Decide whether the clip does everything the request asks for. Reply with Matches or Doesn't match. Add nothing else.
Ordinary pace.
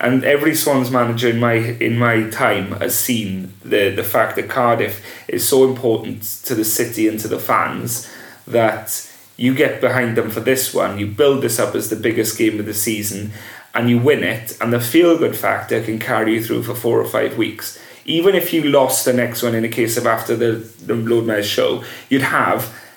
Doesn't match